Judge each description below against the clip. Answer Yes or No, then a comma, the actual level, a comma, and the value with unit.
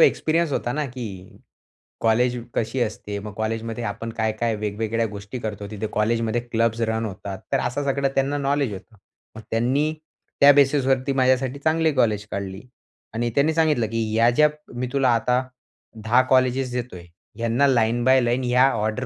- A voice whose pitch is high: No, low, 120 Hz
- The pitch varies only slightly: No, average, 3.2 semitones